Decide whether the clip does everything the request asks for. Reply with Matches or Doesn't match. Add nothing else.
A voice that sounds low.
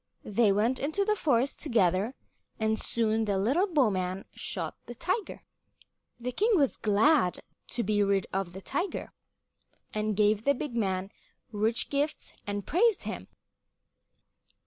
Doesn't match